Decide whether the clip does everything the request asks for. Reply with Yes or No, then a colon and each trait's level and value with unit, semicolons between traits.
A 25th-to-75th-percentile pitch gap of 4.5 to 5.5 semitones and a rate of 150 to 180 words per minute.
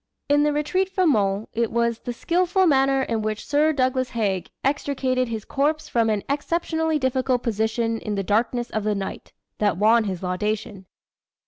Yes: average, 5.2 semitones; average, 170 wpm